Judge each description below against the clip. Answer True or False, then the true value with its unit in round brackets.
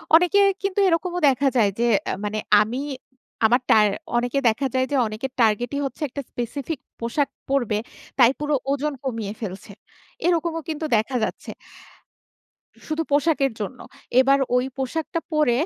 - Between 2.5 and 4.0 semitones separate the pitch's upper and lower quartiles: False (4.4 semitones)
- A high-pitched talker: True (265 Hz)